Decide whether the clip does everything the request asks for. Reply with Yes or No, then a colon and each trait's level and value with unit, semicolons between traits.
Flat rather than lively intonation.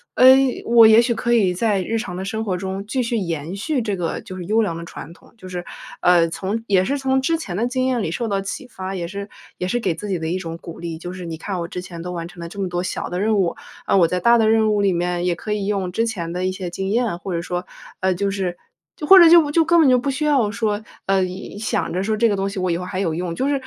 No: average, 4.2 semitones